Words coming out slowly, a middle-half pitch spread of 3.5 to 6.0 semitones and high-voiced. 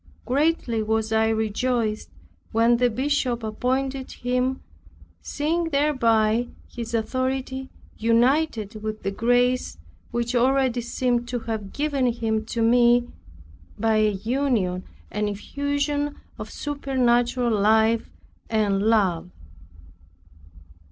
No: slow, 105 wpm; average, 3.0 semitones; high, 240 Hz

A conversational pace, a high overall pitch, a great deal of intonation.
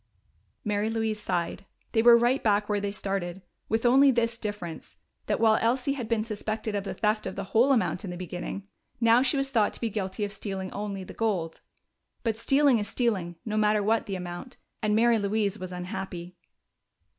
No: average, 195 wpm; high, 210 Hz; average, 3.0 semitones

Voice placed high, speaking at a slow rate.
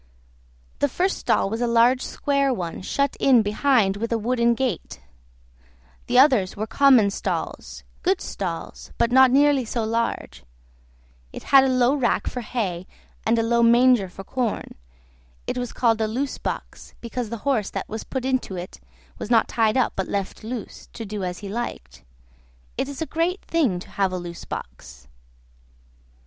No: high, 235 Hz; average, 175 wpm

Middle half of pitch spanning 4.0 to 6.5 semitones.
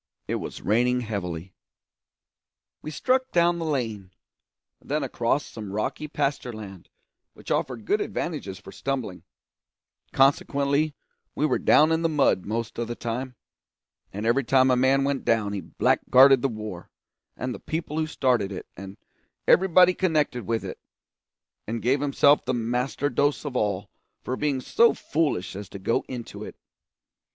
Yes: average, 5.1 semitones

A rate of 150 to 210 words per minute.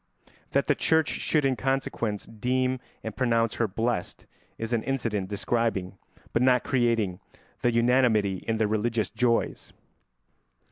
No: slow, 135 wpm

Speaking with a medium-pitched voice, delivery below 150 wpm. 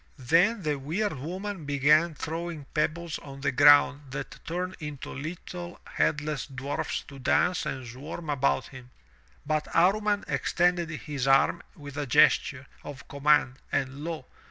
Yes: medium, 150 Hz; average, 140 wpm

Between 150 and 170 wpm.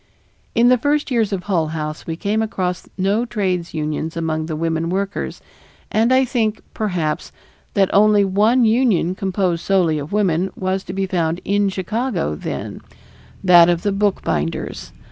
Yes: average, 160 wpm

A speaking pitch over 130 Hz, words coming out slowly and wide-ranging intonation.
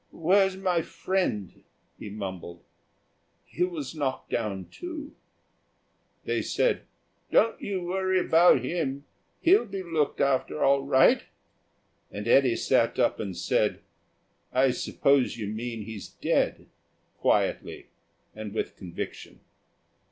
Yes: medium, 140 Hz; slow, 115 wpm; wide, 8.9 semitones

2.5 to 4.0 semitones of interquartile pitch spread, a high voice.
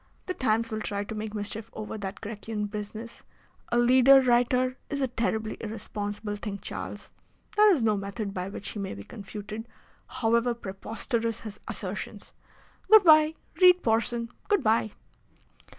Yes: average, 2.9 semitones; high, 225 Hz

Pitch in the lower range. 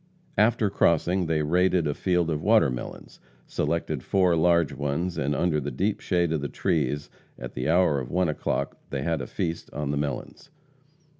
Yes: very low, 80 Hz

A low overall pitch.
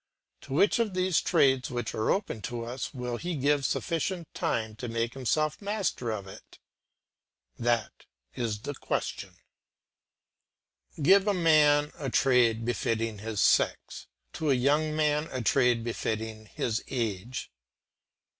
Yes: low, 125 Hz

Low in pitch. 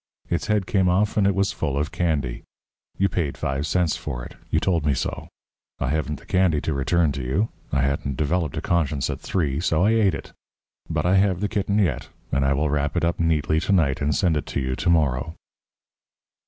Yes: very low, 80 Hz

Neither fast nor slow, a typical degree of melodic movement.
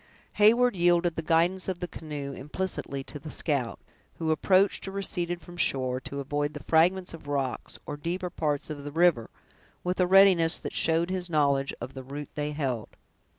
Yes: average, 190 wpm; average, 3.8 semitones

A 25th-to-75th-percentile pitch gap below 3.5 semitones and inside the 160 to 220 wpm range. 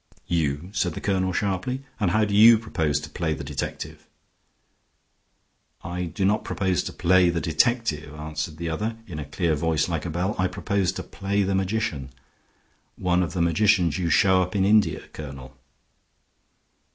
No: average, 3.8 semitones; average, 170 wpm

